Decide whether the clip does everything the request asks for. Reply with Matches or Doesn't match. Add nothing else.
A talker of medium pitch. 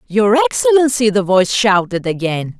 Doesn't match